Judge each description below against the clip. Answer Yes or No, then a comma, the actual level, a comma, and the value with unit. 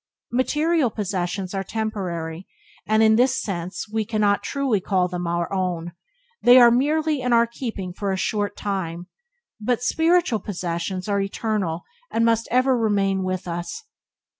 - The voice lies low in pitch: No, high, 210 Hz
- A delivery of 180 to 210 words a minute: No, average, 160 wpm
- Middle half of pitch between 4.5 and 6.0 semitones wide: Yes, average, 4.9 semitones